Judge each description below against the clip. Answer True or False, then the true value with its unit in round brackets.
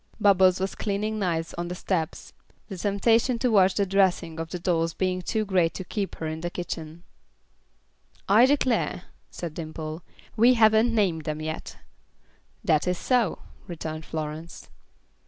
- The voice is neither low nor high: True (180 Hz)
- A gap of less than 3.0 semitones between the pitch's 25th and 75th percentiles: False (4.3 semitones)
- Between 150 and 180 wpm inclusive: True (155 wpm)